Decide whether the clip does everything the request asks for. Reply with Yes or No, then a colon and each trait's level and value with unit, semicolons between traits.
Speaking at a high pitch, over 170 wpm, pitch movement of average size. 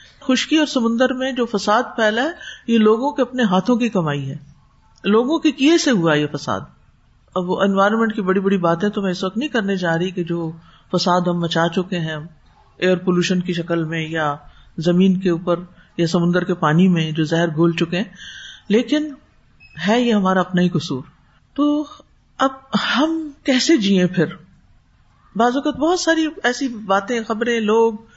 No: high, 195 Hz; average, 185 wpm; wide, 6.1 semitones